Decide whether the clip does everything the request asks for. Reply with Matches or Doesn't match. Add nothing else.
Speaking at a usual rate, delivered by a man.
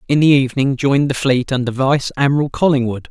Matches